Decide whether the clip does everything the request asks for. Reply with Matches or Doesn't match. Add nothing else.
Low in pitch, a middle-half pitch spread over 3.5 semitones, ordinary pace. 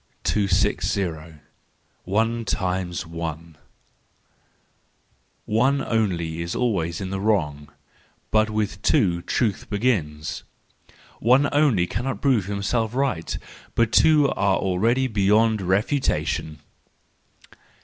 Doesn't match